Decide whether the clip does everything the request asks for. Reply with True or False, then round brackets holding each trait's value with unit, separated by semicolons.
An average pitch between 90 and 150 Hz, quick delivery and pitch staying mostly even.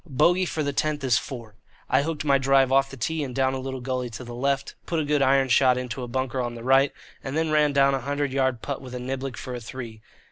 True (135 Hz; 270 wpm; 1.9 semitones)